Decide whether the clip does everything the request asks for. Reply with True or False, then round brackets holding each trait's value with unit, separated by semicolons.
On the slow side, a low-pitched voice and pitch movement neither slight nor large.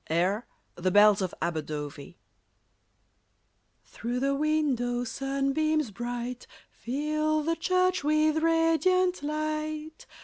False (95 wpm; 285 Hz; 4.7 semitones)